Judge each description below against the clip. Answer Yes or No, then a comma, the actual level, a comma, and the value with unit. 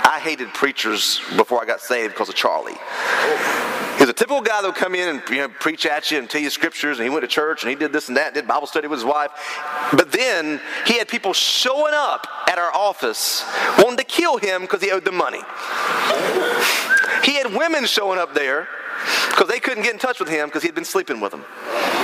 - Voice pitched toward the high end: Yes, high, 200 Hz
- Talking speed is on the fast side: Yes, fast, 230 wpm